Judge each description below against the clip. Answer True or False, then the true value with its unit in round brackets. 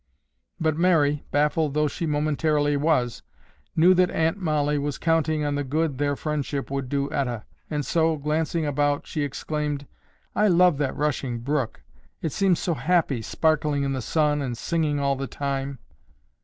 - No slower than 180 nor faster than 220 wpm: False (165 wpm)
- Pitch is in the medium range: True (150 Hz)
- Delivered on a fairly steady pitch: True (2.2 semitones)